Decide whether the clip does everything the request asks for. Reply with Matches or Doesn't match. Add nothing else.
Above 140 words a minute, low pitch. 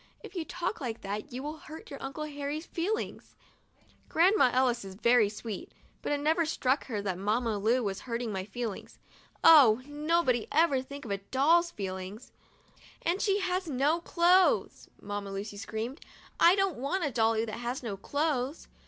Doesn't match